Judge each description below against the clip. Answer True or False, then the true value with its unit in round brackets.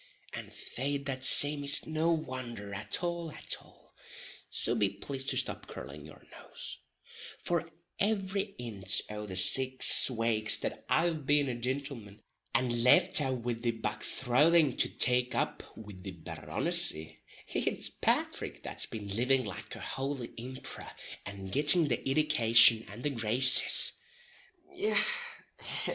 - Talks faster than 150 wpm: False (140 wpm)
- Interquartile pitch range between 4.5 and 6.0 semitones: True (5.2 semitones)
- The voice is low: True (125 Hz)